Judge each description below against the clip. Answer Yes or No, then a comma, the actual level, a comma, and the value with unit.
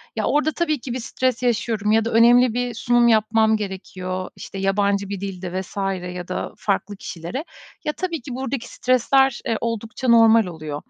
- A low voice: No, high, 225 Hz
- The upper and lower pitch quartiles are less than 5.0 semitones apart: Yes, average, 4.0 semitones